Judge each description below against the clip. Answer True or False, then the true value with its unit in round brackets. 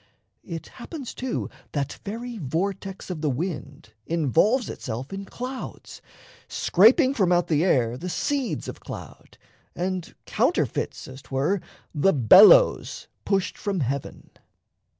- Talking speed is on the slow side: True (125 wpm)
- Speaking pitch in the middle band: True (180 Hz)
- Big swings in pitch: True (6.7 semitones)